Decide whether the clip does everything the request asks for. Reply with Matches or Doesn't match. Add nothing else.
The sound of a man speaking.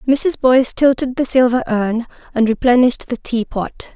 Doesn't match